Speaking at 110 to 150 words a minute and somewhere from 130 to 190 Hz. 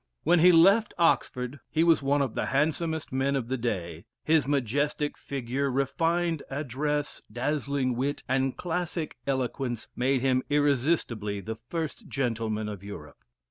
Yes: average, 140 wpm; medium, 140 Hz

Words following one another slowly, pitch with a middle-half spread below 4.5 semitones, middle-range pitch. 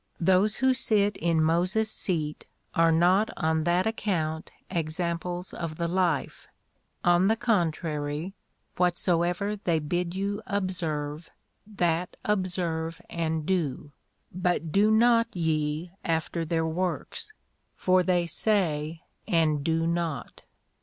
Yes: slow, 115 wpm; average, 2.7 semitones; medium, 175 Hz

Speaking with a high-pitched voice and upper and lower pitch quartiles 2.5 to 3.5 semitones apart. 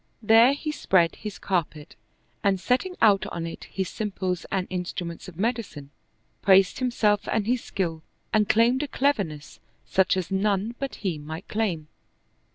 No: high, 195 Hz; average, 4.5 semitones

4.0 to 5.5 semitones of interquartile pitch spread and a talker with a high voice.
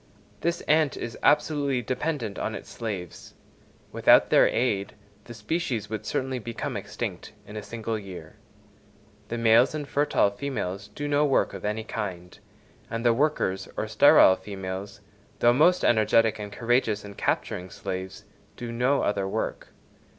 No: average, 4.6 semitones; low, 115 Hz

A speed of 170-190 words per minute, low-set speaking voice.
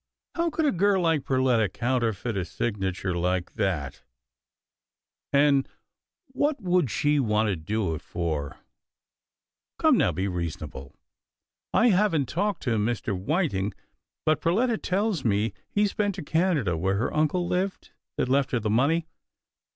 No: average, 150 wpm; low, 130 Hz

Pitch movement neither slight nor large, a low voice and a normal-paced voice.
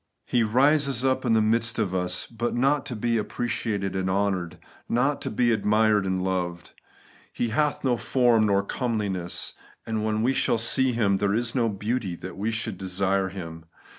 Yes: average, 3.7 semitones; low, 110 Hz; average, 185 wpm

